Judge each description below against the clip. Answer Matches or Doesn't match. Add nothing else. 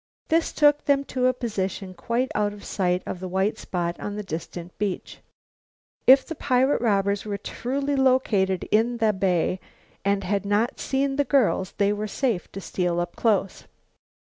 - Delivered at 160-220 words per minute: Matches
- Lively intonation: Doesn't match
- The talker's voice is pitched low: Doesn't match